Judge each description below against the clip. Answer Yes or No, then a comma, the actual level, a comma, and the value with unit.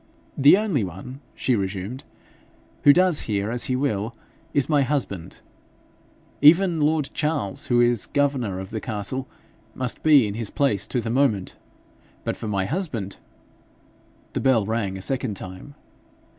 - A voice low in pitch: Yes, low, 120 Hz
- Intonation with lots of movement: Yes, wide, 5.9 semitones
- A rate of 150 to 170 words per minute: Yes, average, 155 wpm